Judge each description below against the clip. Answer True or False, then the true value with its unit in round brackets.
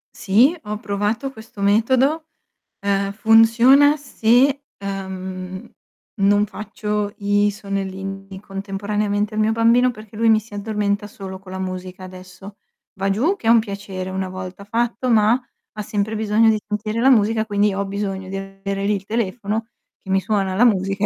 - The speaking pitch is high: True (205 Hz)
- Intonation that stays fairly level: True (2.3 semitones)